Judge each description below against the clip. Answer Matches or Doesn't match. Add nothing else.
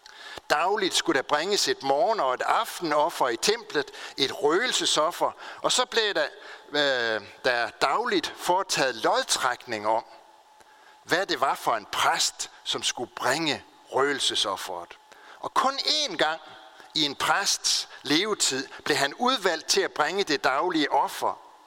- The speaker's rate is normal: Doesn't match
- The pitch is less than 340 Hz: Doesn't match